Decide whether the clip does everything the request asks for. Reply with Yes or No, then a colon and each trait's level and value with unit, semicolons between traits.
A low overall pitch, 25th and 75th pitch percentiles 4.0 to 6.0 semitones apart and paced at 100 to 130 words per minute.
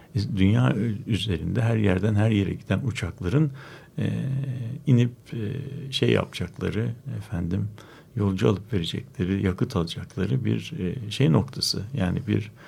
Yes: low, 110 Hz; average, 4.9 semitones; average, 120 wpm